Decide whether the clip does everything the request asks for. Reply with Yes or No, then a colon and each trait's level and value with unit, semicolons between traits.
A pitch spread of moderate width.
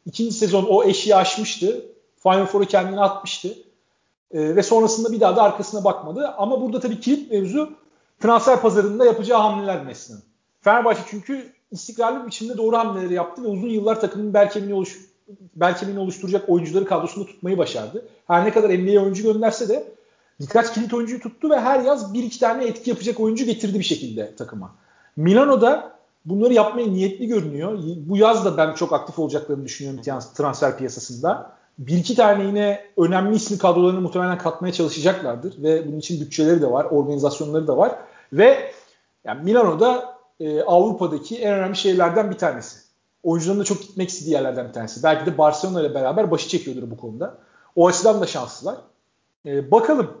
Yes: average, 5.0 semitones